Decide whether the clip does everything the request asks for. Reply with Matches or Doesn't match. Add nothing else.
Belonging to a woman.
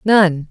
Matches